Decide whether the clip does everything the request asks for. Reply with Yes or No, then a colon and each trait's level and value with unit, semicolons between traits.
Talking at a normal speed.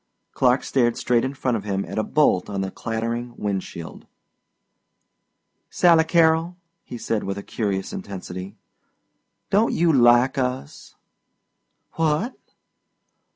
No: slow, 125 wpm